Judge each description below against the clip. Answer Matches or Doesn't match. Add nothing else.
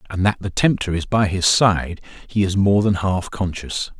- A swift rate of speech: Matches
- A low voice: Matches